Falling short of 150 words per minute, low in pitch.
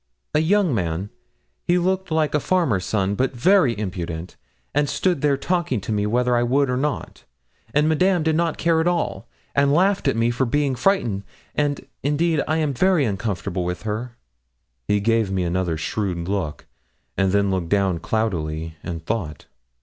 No: average, 175 wpm; low, 120 Hz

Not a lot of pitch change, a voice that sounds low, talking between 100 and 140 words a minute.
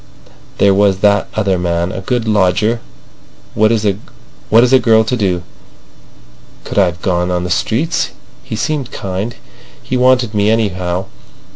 No: average, 3.8 semitones; low, 105 Hz; slow, 135 wpm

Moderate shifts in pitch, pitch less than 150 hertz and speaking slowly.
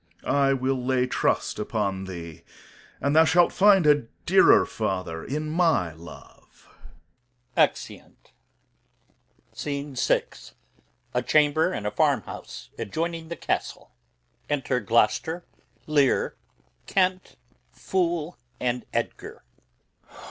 No: wide, 6.2 semitones; medium, 140 Hz; slow, 95 wpm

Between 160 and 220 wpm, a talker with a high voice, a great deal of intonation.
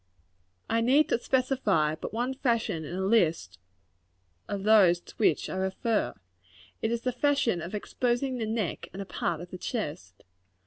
Yes: average, 175 wpm; high, 215 Hz; wide, 5.7 semitones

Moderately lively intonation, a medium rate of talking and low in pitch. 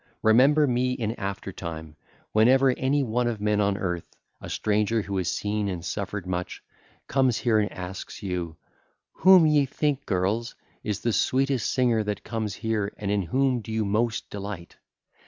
Yes: average, 4.0 semitones; average, 175 wpm; low, 105 Hz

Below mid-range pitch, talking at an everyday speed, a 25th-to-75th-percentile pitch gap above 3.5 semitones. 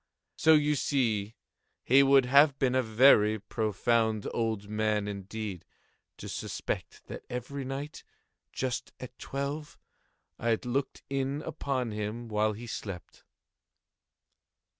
No: low, 120 Hz; slow, 120 wpm; average, 4.2 semitones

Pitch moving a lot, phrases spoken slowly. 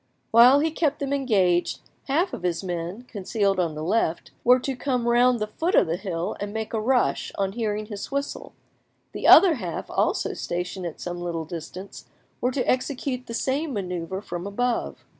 No: wide, 6.0 semitones; average, 185 wpm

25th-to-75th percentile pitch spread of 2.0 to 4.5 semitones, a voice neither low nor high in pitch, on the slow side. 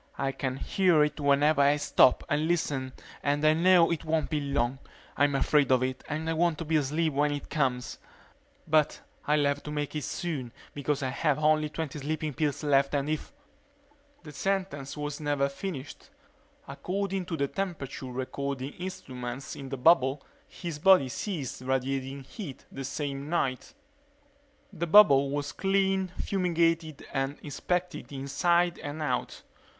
No: average, 3.1 semitones; medium, 145 Hz; average, 160 wpm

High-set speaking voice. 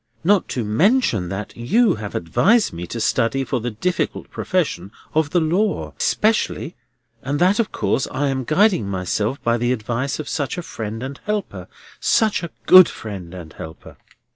No: low, 135 Hz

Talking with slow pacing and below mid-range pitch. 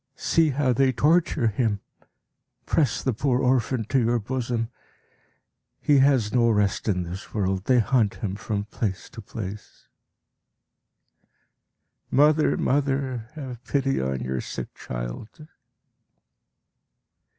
Yes: slow, 115 wpm; low, 120 Hz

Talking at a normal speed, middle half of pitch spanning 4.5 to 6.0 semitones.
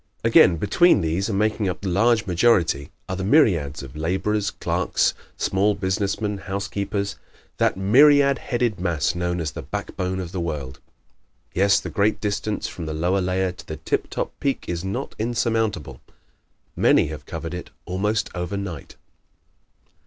No: average, 160 wpm; average, 3.4 semitones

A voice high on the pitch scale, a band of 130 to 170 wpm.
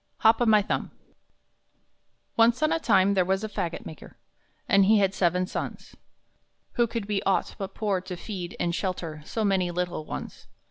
No: high, 195 Hz; average, 180 wpm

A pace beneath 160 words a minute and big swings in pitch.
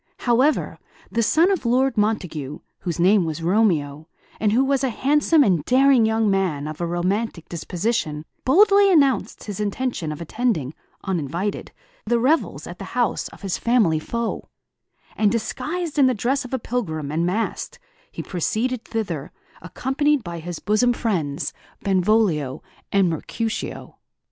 Yes: average, 150 wpm; wide, 6.8 semitones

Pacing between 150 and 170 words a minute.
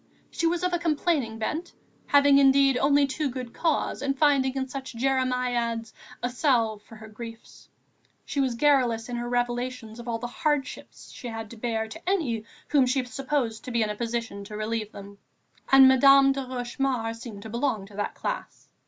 No: average, 180 wpm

